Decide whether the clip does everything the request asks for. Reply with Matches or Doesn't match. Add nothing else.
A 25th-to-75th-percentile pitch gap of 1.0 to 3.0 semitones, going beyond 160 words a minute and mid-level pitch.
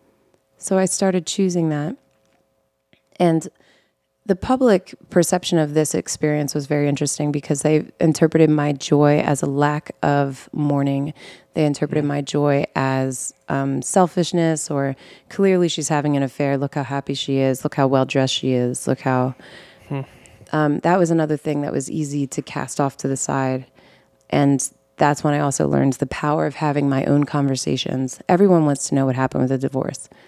Matches